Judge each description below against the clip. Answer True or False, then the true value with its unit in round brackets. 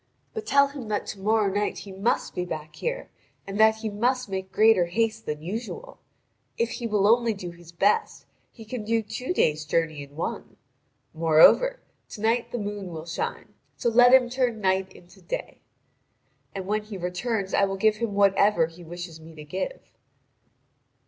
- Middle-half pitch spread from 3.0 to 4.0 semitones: False (4.5 semitones)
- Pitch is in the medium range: False (205 Hz)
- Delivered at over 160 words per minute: True (180 wpm)